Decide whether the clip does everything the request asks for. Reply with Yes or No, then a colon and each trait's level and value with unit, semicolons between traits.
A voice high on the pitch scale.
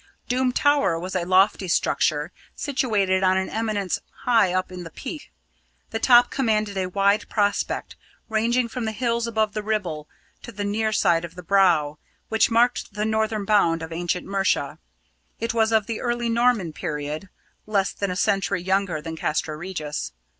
Yes: high, 200 Hz